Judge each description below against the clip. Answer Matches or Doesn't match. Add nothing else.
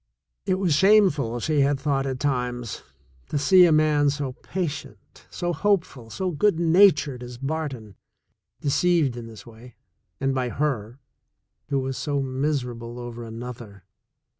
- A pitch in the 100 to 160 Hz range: Matches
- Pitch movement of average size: Matches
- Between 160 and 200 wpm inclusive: Doesn't match